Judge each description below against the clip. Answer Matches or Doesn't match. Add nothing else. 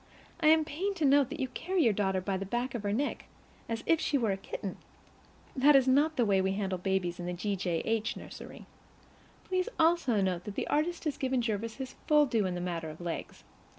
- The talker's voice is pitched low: Doesn't match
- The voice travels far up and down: Matches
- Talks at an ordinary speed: Doesn't match